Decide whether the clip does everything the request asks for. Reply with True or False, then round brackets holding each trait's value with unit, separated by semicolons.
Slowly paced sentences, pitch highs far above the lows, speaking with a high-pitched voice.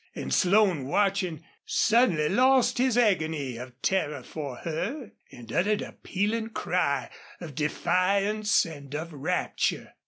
False (125 wpm; 6.0 semitones; 180 Hz)